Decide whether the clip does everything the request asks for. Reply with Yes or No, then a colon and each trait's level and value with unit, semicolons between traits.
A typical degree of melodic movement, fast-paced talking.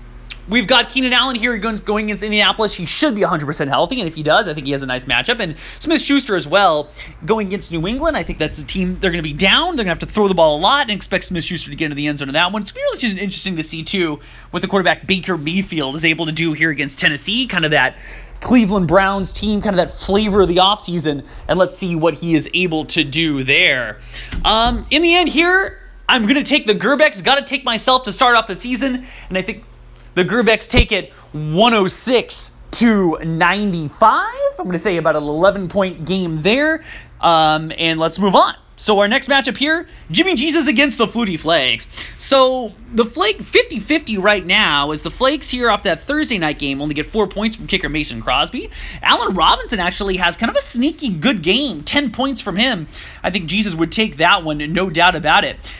No: wide, 6.5 semitones; fast, 225 wpm